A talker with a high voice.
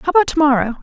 Yes: very high, 295 Hz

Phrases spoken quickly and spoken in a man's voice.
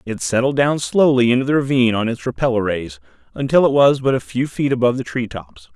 Yes: fast, 230 wpm; male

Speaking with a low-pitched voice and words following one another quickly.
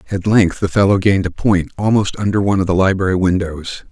Yes: very low, 95 Hz; fast, 215 wpm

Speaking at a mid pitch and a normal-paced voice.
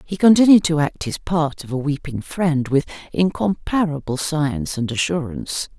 Yes: medium, 160 Hz; average, 155 wpm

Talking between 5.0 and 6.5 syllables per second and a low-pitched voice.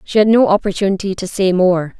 No: 5.9 syllables/s; high, 190 Hz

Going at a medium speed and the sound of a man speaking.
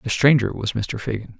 No: fast, 215 wpm; male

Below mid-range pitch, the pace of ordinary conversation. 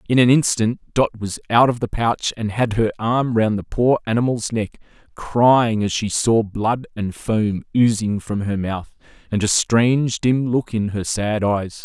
Yes: low, 110 Hz; average, 195 wpm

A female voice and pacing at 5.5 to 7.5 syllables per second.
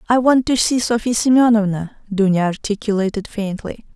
No: female; 5.3 syllables/s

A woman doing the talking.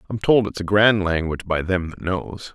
No: male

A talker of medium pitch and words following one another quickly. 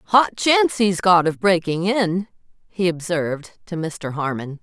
No: medium, 180 Hz; average, 155 wpm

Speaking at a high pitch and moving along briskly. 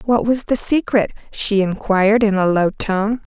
No: high, 210 Hz; average, 180 wpm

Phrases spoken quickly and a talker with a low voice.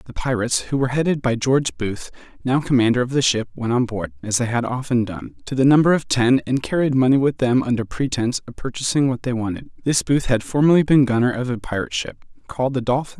Yes: fast, 230 wpm; low, 125 Hz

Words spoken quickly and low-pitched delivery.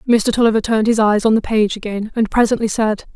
No: fast, 230 wpm; high, 220 Hz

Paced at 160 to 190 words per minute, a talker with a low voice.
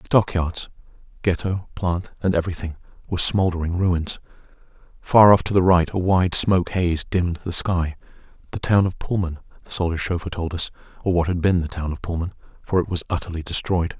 Yes: average, 180 wpm; very low, 90 Hz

